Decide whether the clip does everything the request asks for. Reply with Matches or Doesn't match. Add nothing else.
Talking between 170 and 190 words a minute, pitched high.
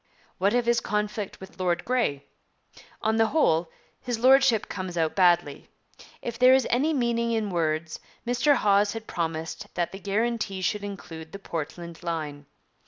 Doesn't match